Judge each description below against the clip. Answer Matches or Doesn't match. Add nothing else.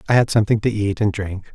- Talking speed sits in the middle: Doesn't match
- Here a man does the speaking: Matches